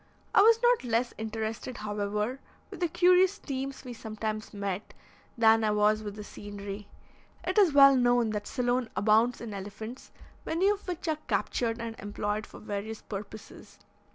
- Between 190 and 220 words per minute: No, average, 160 wpm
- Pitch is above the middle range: Yes, high, 225 Hz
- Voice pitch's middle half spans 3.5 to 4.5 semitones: Yes, average, 4.0 semitones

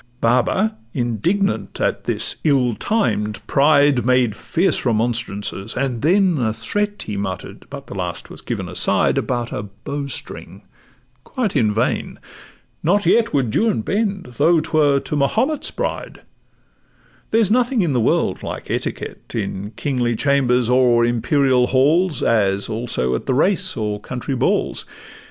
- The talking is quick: No, average, 140 wpm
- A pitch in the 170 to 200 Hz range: No, low, 130 Hz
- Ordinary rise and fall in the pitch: No, wide, 6.9 semitones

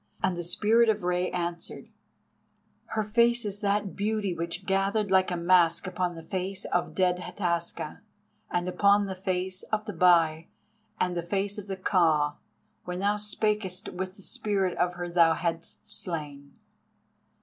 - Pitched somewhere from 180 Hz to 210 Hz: Yes, medium, 185 Hz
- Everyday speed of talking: Yes, average, 160 wpm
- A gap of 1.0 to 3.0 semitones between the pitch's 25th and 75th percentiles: Yes, narrow, 2.6 semitones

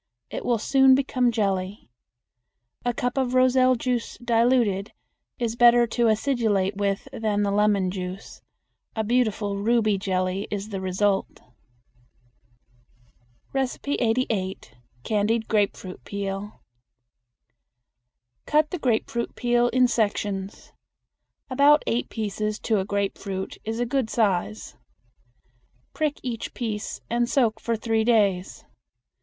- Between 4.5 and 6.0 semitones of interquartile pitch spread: No, average, 3.4 semitones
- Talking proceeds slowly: Yes, slow, 115 wpm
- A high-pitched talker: Yes, high, 220 Hz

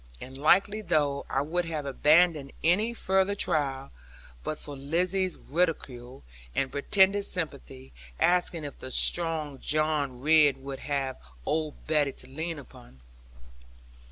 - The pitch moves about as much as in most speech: Yes, average, 4.2 semitones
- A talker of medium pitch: Yes, medium, 150 Hz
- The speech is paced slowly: Yes, slow, 130 wpm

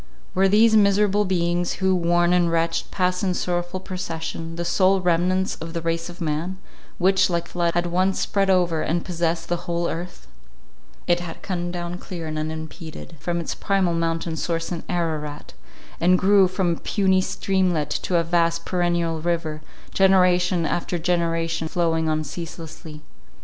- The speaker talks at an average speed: Yes, average, 165 wpm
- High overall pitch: No, medium, 175 Hz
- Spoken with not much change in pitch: Yes, narrow, 1.8 semitones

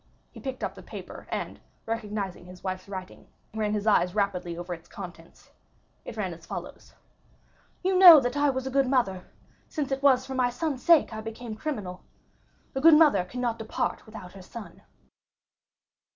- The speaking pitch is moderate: No, high, 225 Hz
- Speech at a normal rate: Yes, average, 175 wpm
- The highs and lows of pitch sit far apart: Yes, wide, 6.1 semitones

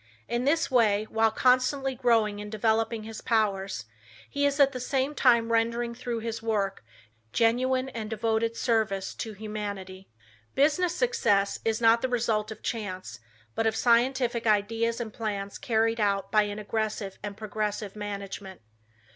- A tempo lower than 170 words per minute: Yes, average, 150 wpm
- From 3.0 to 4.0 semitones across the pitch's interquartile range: No, narrow, 2.4 semitones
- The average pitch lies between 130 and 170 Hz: No, high, 225 Hz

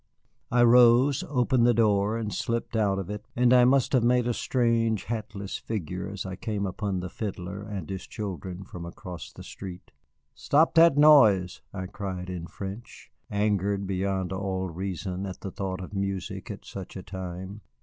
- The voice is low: Yes, low, 100 Hz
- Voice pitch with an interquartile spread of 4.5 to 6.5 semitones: No, average, 3.7 semitones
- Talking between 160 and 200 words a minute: Yes, average, 175 wpm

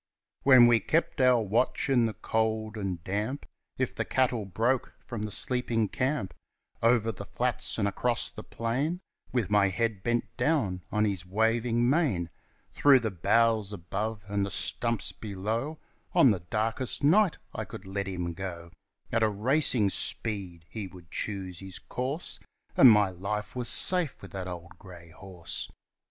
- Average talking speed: Yes, average, 160 wpm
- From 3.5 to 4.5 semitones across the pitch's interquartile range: Yes, average, 4.0 semitones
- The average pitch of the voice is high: No, low, 110 Hz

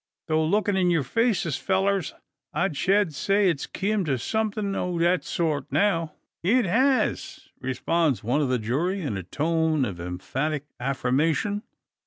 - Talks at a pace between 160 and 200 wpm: No, average, 150 wpm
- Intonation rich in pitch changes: Yes, wide, 6.1 semitones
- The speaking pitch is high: No, medium, 165 Hz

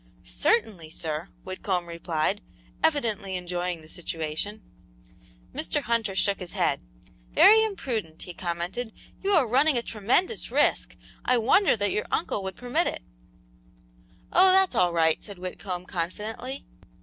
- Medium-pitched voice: No, high, 200 Hz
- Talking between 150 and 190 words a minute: No, slow, 135 wpm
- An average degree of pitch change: No, wide, 6.2 semitones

